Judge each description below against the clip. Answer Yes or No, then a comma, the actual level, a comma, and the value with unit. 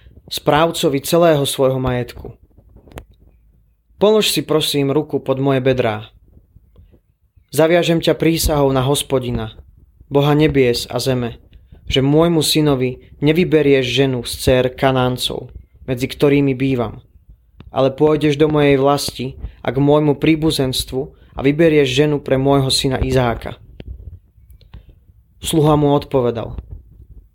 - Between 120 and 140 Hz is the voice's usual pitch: Yes, low, 135 Hz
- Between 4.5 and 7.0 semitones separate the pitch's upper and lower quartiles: Yes, average, 4.8 semitones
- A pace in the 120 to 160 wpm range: No, slow, 110 wpm